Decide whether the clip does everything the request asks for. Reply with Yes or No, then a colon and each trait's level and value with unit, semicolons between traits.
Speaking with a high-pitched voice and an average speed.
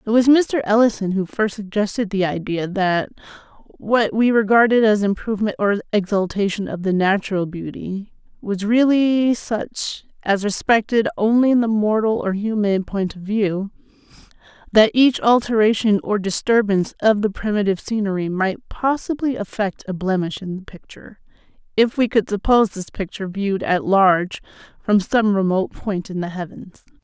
Yes: high, 210 Hz; average, 150 wpm